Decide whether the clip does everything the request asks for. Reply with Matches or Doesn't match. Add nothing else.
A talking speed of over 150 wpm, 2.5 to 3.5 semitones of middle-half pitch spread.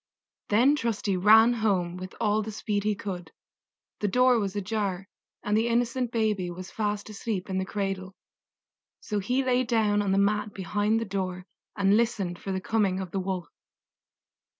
Matches